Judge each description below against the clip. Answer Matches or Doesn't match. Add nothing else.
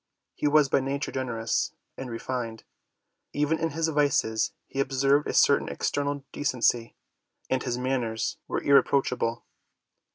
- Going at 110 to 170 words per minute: Matches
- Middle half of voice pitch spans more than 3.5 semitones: Doesn't match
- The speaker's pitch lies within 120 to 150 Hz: Matches